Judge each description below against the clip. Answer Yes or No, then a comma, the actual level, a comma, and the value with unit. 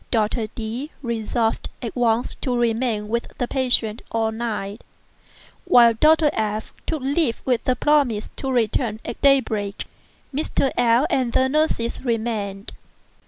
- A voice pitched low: No, high, 235 Hz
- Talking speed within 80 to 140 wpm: Yes, slow, 135 wpm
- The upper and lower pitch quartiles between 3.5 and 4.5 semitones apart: No, average, 3.0 semitones